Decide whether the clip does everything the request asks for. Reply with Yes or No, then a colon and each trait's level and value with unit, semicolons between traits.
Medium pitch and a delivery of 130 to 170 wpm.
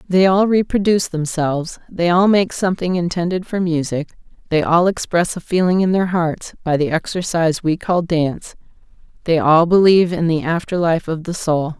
No: medium, 170 Hz; average, 180 wpm